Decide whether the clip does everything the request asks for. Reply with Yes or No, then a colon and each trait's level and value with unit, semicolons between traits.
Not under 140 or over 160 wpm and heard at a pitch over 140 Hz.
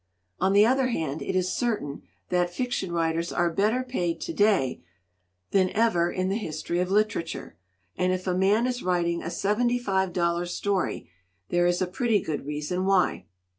No: average, 175 wpm; medium, 185 Hz